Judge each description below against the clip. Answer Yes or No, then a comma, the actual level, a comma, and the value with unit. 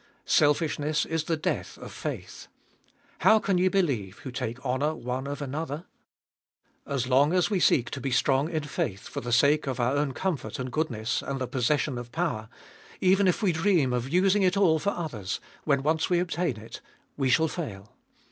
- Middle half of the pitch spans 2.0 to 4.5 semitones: No, average, 5.1 semitones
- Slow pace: No, average, 195 wpm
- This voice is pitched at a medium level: Yes, medium, 145 Hz